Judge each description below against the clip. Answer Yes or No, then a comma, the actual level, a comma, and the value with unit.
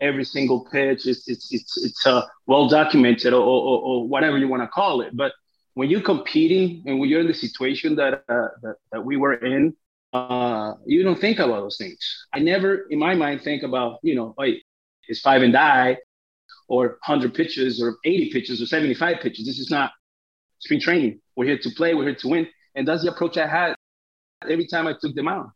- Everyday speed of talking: No, fast, 215 wpm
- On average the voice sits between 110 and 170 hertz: Yes, medium, 140 Hz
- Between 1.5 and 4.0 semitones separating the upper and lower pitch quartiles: No, average, 4.7 semitones